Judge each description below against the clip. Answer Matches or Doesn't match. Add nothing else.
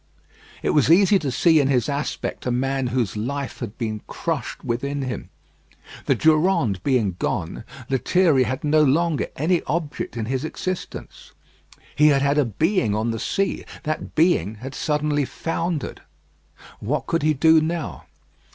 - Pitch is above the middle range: Doesn't match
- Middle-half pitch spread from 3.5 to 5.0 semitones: Matches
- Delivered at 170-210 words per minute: Doesn't match